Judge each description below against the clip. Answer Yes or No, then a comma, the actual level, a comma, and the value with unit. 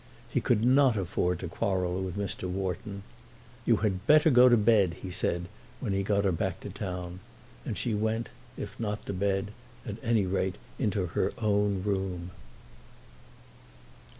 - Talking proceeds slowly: No, average, 160 wpm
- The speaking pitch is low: Yes, low, 100 Hz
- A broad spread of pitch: No, average, 2.7 semitones